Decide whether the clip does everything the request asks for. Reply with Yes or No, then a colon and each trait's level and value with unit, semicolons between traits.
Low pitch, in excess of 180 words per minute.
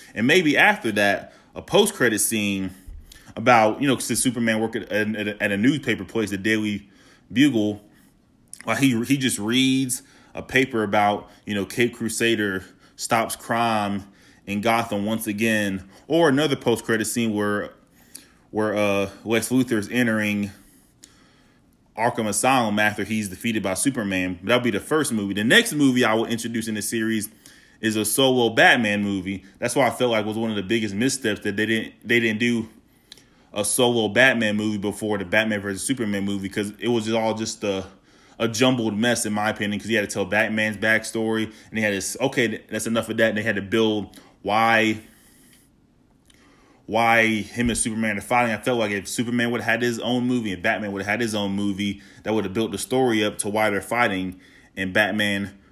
Yes: low, 110 Hz; average, 190 wpm